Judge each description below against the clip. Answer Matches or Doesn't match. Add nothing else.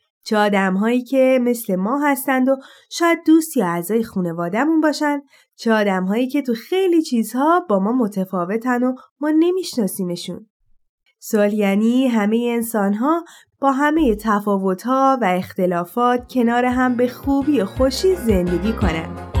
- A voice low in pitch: Doesn't match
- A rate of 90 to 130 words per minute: Doesn't match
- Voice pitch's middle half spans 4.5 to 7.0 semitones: Matches